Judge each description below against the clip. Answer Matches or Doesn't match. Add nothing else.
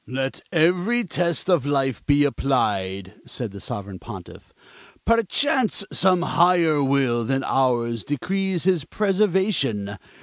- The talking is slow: Matches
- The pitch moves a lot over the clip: Matches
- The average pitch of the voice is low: Doesn't match